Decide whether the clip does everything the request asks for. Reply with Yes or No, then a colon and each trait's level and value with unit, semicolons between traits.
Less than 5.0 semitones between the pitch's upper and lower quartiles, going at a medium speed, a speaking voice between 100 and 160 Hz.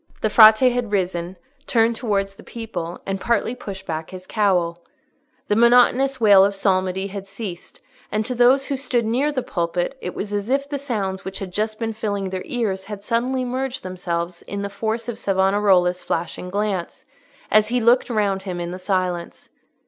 No: average, 3.9 semitones; average, 185 wpm; high, 205 Hz